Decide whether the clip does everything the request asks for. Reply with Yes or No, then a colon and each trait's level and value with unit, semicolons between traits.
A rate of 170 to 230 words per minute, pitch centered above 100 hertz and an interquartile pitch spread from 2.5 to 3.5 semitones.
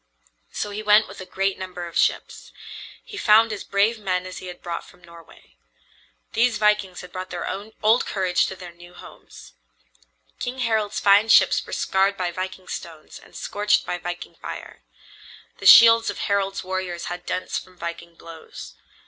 Yes: average, 175 wpm; medium, 185 Hz; average, 2.9 semitones